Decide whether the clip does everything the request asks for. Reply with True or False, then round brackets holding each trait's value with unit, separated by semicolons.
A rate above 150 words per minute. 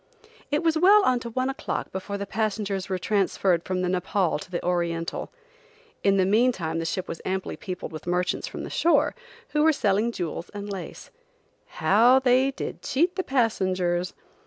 True (180 wpm)